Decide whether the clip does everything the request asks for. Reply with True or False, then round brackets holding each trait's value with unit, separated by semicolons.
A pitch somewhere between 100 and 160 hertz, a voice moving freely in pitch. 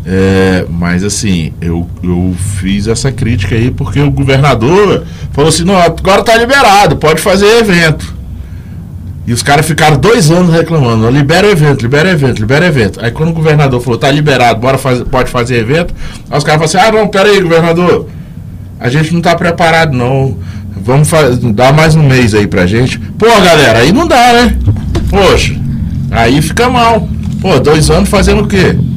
True (135 Hz; 7.7 semitones)